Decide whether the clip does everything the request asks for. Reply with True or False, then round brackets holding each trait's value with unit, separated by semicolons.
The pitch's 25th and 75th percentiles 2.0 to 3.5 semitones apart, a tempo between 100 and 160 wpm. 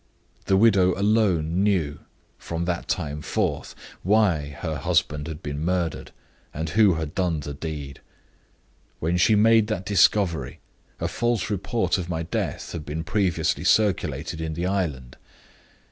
False (4.3 semitones; 145 wpm)